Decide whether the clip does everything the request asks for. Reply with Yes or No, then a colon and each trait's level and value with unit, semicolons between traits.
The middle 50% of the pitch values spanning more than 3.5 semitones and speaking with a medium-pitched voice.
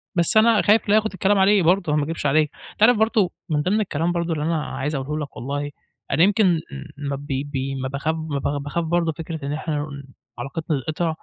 Yes: average, 4.1 semitones; medium, 160 Hz